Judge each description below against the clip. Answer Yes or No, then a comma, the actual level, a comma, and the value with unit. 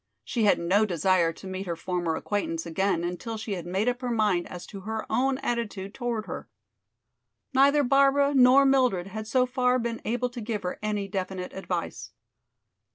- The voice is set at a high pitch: Yes, high, 215 Hz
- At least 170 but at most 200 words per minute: Yes, average, 180 wpm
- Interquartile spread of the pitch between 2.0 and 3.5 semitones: No, average, 5.0 semitones